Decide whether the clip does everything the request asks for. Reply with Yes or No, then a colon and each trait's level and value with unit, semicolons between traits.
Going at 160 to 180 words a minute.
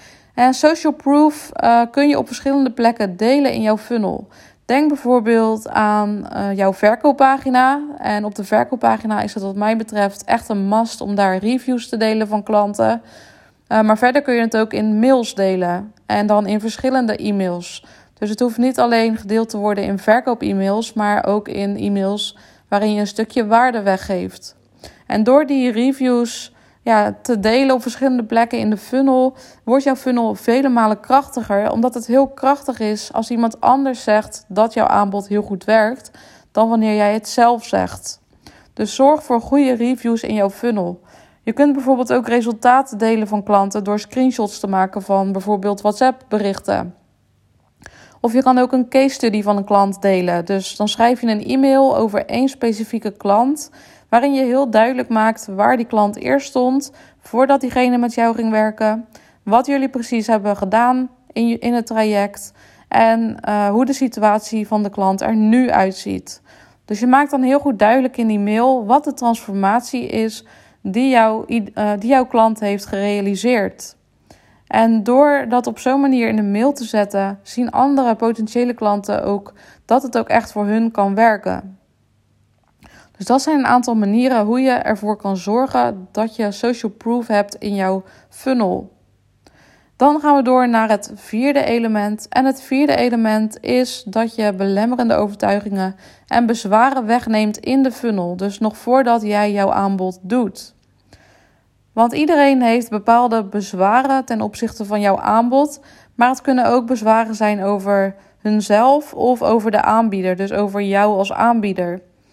Yes: average, 170 wpm